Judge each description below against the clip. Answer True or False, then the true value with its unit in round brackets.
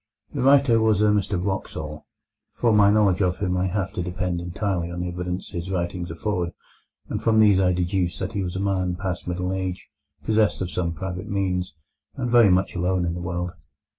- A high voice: False (90 Hz)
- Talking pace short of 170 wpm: False (200 wpm)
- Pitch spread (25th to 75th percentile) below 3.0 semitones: True (2.4 semitones)